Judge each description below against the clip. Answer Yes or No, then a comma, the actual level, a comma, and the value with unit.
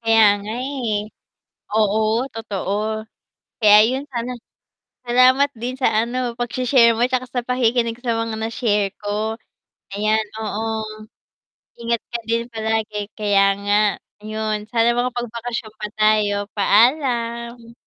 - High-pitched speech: Yes, high, 230 Hz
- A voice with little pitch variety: Yes, narrow, 2.1 semitones